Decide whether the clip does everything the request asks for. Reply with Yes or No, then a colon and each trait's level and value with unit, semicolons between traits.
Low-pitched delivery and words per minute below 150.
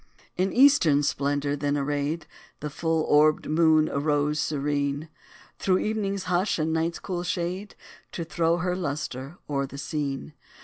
No: medium, 155 Hz; average, 140 wpm